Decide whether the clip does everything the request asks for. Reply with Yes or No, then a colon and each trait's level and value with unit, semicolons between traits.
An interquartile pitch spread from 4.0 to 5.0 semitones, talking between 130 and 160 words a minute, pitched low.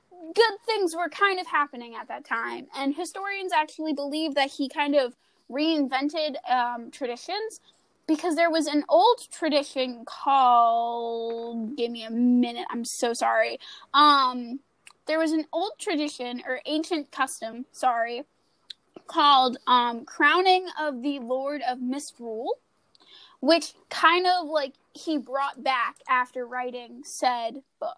No: average, 4.7 semitones; slow, 135 wpm; very high, 290 Hz